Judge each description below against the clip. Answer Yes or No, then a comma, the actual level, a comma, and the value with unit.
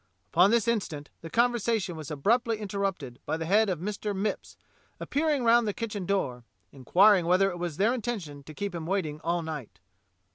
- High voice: Yes, high, 195 Hz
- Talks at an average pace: Yes, average, 185 wpm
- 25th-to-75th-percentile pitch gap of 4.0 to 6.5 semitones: Yes, wide, 5.4 semitones